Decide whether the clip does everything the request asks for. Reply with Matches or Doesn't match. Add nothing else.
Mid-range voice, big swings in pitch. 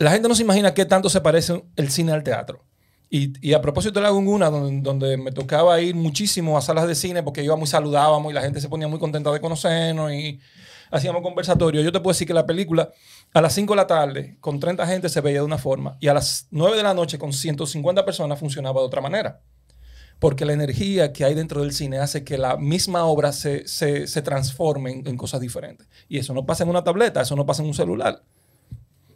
Doesn't match